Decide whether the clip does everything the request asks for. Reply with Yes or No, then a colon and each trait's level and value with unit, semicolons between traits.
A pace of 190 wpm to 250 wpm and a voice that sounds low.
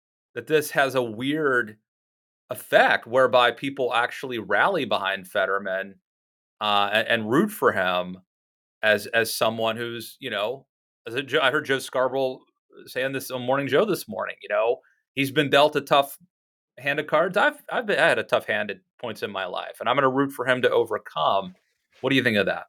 Yes: average, 200 wpm; low, 125 Hz